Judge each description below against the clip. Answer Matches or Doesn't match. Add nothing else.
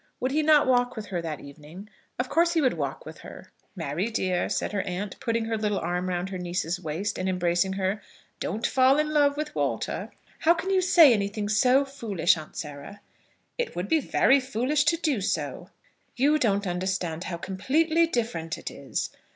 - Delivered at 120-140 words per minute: Doesn't match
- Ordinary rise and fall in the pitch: Doesn't match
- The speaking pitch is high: Matches